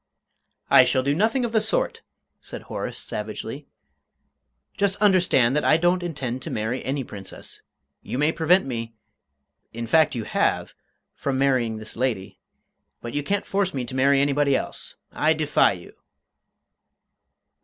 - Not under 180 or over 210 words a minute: No, average, 150 wpm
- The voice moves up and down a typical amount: No, wide, 6.2 semitones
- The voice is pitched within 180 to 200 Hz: No, medium, 140 Hz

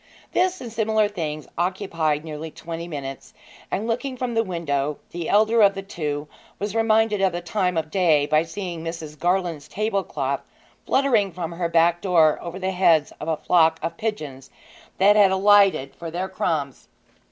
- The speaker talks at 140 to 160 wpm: No, average, 175 wpm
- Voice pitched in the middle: Yes, medium, 175 Hz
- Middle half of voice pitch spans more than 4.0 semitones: Yes, average, 4.5 semitones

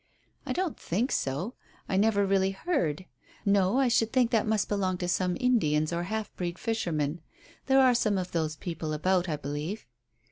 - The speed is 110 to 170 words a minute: No, average, 180 wpm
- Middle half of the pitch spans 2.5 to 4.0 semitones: No, average, 4.8 semitones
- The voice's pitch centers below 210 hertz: Yes, high, 190 Hz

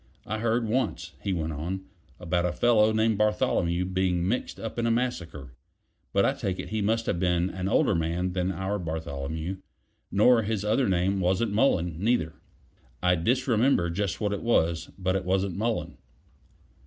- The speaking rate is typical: Yes, average, 170 wpm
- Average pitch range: Yes, average, 4.0 semitones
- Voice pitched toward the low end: Yes, very low, 95 Hz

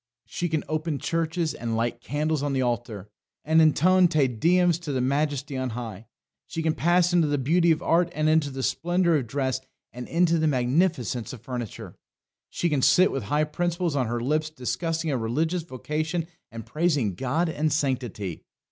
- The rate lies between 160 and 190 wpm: Yes, average, 180 wpm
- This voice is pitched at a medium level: Yes, medium, 150 Hz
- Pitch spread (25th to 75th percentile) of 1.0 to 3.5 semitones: No, average, 4.5 semitones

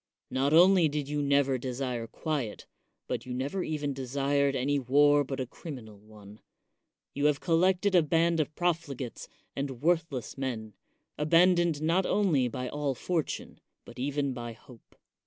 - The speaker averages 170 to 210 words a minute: No, average, 150 wpm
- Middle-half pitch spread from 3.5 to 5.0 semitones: Yes, average, 4.1 semitones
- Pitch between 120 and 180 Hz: Yes, medium, 140 Hz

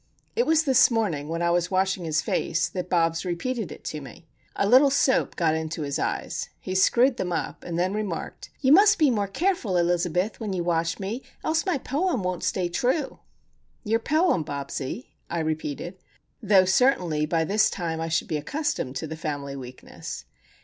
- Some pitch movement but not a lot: No, wide, 7.0 semitones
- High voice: No, medium, 180 Hz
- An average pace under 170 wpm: No, average, 185 wpm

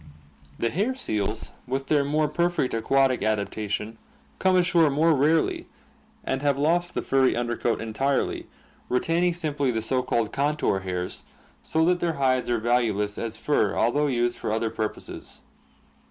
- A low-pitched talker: Yes, low, 130 Hz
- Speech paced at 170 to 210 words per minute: No, average, 155 wpm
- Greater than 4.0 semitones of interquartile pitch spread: Yes, wide, 5.4 semitones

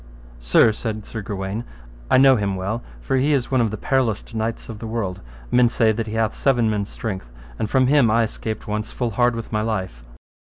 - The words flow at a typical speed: No, fast, 215 wpm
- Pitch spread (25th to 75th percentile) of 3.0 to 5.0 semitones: No, narrow, 2.5 semitones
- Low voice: Yes, low, 110 Hz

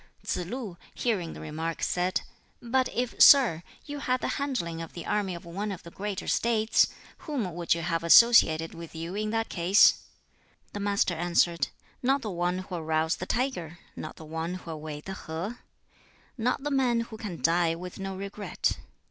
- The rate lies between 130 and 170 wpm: No, average, 180 wpm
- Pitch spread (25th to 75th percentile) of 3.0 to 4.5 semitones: No, average, 5.3 semitones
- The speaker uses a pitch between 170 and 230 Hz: Yes, medium, 185 Hz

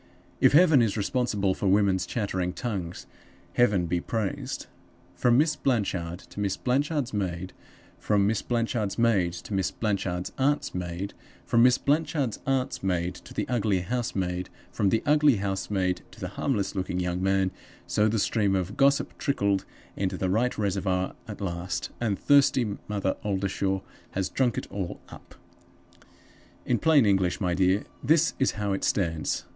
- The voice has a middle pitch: No, low, 100 Hz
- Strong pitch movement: No, average, 4.4 semitones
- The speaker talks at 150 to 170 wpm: Yes, average, 155 wpm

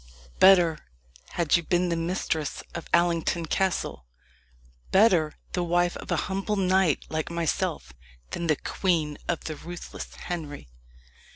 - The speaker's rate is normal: No, slow, 130 wpm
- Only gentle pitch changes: Yes, narrow, 2.3 semitones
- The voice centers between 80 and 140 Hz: No, medium, 170 Hz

